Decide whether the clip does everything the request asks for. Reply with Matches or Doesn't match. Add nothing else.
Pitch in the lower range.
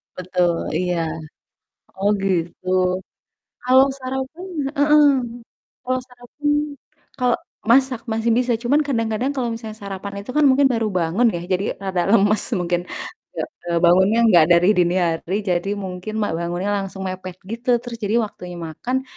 Doesn't match